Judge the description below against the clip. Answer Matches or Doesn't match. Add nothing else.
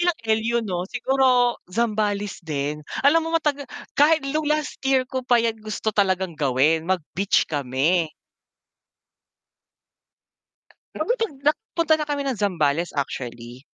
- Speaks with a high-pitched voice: Matches